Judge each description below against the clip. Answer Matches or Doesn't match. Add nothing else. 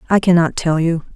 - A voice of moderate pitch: Matches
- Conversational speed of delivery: Doesn't match